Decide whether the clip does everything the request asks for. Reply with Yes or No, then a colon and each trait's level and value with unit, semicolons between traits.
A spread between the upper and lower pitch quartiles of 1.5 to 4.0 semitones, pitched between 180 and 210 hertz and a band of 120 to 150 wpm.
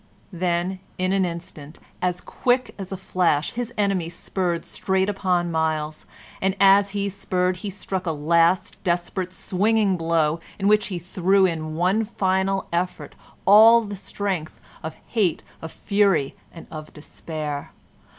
Yes: average, 2.9 semitones; medium, 185 Hz; average, 145 wpm